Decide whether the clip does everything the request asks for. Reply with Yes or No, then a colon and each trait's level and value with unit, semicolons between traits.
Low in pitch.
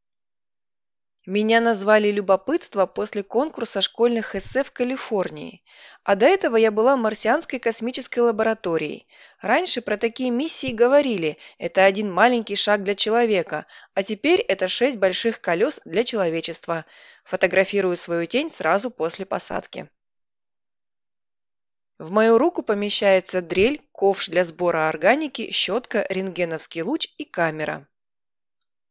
No: high, 205 Hz